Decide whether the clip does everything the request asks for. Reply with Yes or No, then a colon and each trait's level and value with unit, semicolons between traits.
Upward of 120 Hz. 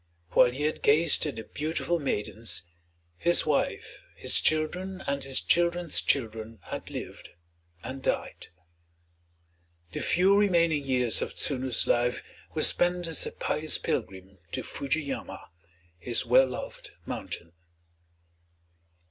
Yes: medium, 140 Hz